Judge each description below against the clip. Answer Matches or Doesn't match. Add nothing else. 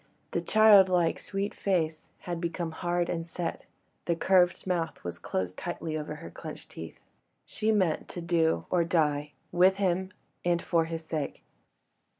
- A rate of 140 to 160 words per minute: Matches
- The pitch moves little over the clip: Matches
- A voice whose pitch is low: Doesn't match